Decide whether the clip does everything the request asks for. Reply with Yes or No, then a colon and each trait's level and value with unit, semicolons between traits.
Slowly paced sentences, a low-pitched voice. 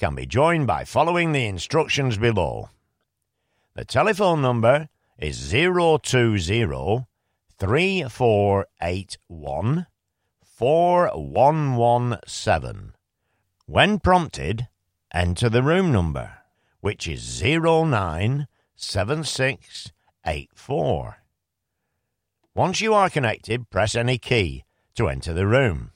Yes: slow, 80 wpm; low, 120 Hz